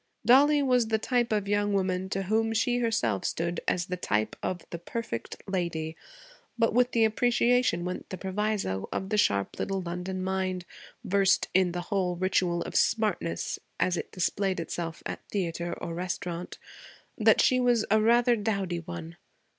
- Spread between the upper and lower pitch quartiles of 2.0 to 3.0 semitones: No, average, 4.2 semitones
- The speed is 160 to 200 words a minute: Yes, average, 165 wpm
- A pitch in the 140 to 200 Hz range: Yes, high, 190 Hz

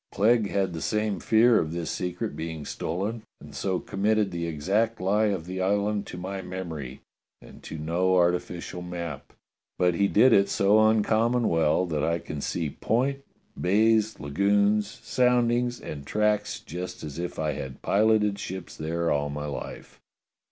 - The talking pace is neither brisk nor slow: Yes, average, 165 wpm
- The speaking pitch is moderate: No, very low, 95 Hz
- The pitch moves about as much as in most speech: Yes, average, 4.3 semitones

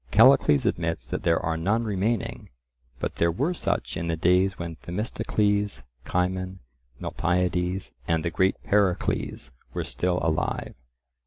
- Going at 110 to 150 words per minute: Yes, slow, 135 wpm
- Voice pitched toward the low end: Yes, very low, 90 Hz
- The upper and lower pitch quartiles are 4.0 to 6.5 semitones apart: No, average, 3.4 semitones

